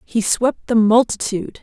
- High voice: Yes, high, 225 Hz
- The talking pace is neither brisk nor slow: Yes, average, 150 wpm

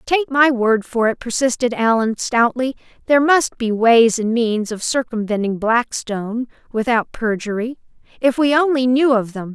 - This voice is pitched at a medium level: No, high, 240 Hz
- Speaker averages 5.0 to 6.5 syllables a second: No, 4.4 syllables/s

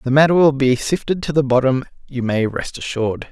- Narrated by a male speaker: Yes, male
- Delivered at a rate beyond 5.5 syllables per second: Yes, 5.7 syllables/s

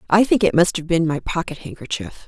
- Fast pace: Yes, fast, 240 wpm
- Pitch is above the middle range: No, medium, 170 Hz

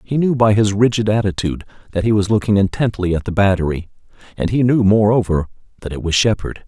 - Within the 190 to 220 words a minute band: Yes, average, 200 wpm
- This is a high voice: No, low, 100 Hz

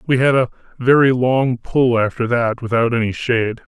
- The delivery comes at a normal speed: Yes, average, 175 wpm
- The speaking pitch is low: Yes, low, 120 Hz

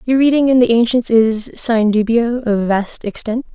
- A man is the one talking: No, female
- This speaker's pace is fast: No, average, 185 wpm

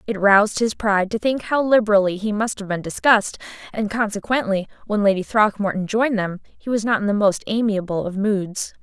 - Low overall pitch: No, high, 210 Hz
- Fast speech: No, average, 195 wpm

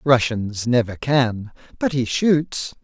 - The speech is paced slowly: Yes, slow, 125 wpm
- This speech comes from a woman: No, male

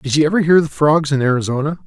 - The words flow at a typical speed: No, fast, 260 wpm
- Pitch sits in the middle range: Yes, medium, 150 Hz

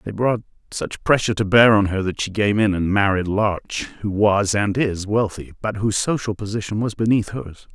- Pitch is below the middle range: Yes, low, 105 Hz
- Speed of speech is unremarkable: No, fast, 210 wpm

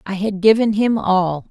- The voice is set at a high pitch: Yes, high, 200 Hz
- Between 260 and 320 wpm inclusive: No, average, 200 wpm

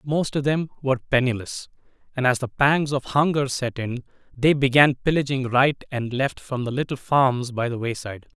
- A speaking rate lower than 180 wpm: No, average, 185 wpm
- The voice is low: Yes, low, 130 Hz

